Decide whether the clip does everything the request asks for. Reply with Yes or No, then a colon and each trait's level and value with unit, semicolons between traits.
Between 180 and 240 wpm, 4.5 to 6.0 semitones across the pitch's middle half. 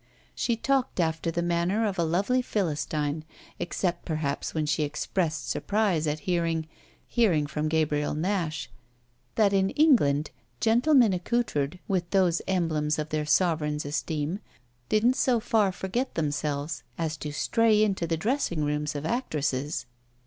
No: average, 140 wpm; average, 5.1 semitones